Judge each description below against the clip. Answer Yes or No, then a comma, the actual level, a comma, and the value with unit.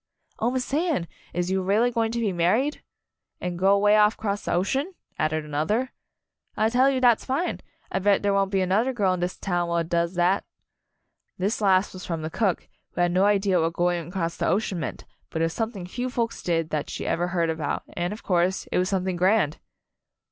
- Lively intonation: No, average, 4.1 semitones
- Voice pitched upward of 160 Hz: Yes, high, 190 Hz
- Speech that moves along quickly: Yes, fast, 215 wpm